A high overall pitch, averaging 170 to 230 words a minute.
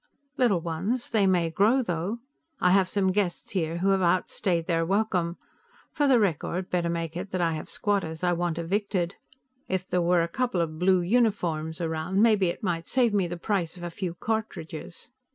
No: medium, 180 Hz; average, 190 wpm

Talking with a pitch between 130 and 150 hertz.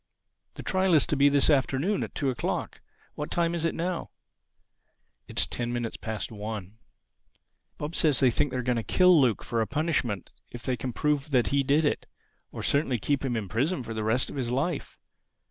Yes: low, 135 Hz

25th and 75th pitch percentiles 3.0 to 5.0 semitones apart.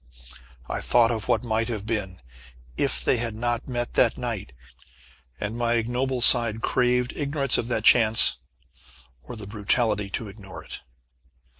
No: narrow, 2.4 semitones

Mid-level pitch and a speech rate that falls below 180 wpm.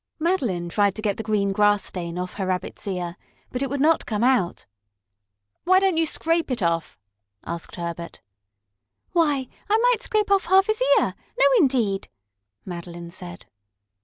No: high, 210 Hz; average, 160 wpm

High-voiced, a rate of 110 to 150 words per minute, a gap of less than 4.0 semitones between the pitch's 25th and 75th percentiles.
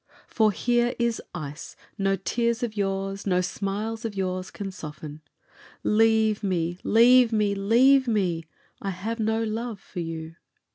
Yes: high, 205 Hz; average, 145 wpm; average, 3.6 semitones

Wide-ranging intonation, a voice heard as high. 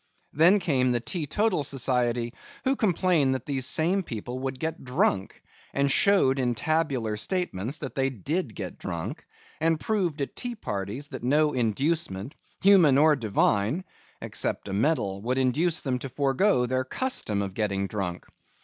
No: wide, 5.7 semitones; low, 135 Hz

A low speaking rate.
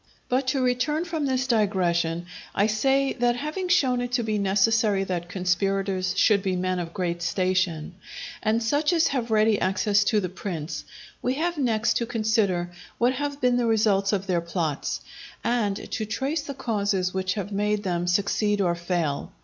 No: average, 175 wpm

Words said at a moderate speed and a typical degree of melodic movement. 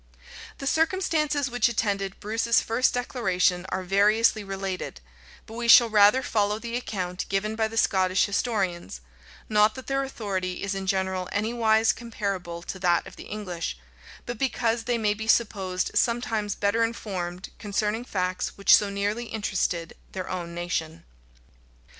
Yes: average, 145 wpm; average, 3.5 semitones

